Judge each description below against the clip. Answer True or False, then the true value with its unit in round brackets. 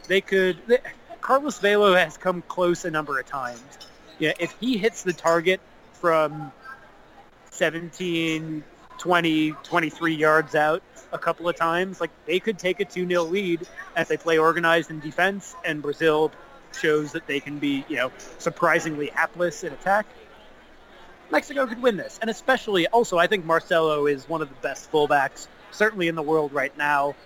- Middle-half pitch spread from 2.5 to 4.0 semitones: True (3.1 semitones)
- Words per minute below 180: True (170 wpm)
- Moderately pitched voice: True (170 Hz)